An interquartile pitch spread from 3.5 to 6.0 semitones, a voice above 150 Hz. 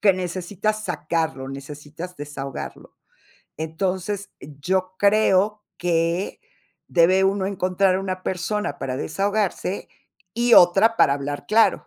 Yes: average, 4.0 semitones; medium, 185 Hz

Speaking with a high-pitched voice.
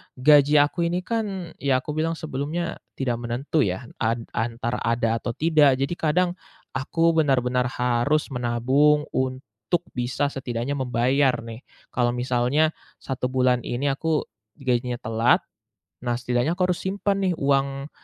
No: low, 135 Hz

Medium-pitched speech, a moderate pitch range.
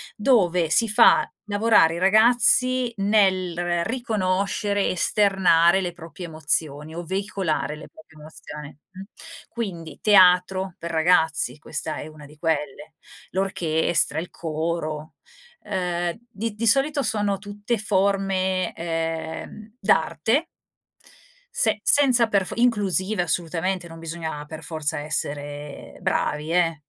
Yes: medium, 180 Hz; average, 4.2 semitones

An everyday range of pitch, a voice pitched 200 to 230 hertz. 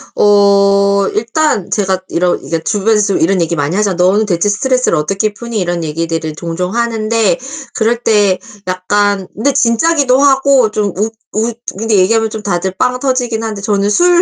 Yes: average, 3.5 semitones; high, 205 Hz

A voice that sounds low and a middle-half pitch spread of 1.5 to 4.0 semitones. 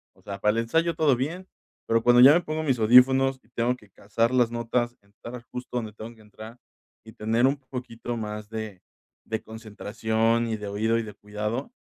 Yes: low, 115 Hz; narrow, 2.6 semitones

